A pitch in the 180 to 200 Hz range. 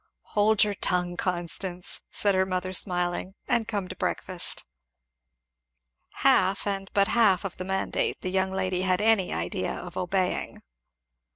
Yes: high, 190 Hz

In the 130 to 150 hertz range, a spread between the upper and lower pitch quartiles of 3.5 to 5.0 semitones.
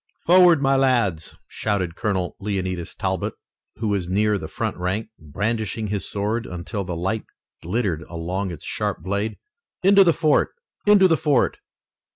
No: low, 105 Hz; average, 4.7 semitones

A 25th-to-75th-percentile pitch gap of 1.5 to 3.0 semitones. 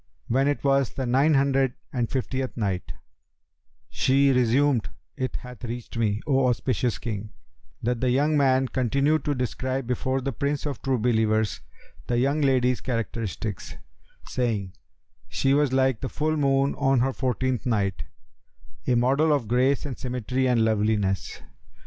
Yes: narrow, 2.6 semitones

